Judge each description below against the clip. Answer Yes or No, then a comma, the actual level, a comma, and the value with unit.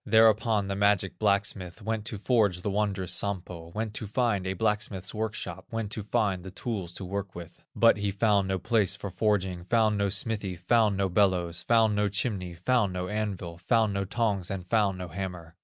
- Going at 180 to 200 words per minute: Yes, average, 190 wpm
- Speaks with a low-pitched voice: Yes, low, 100 Hz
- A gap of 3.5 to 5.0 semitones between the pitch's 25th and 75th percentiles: No, average, 2.7 semitones